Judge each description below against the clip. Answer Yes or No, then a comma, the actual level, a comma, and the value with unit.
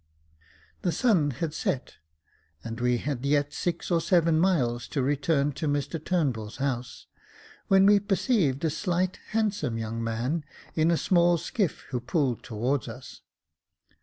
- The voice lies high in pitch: No, medium, 145 Hz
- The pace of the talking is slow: No, average, 145 wpm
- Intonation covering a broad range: Yes, wide, 5.7 semitones